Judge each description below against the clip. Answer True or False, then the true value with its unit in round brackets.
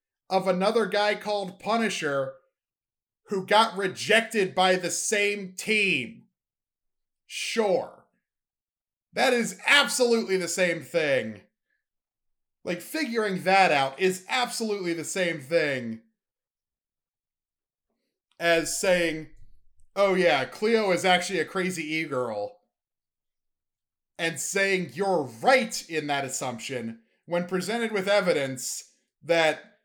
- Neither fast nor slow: False (105 wpm)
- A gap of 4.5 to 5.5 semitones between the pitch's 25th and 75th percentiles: True (5.1 semitones)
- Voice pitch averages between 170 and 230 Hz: True (185 Hz)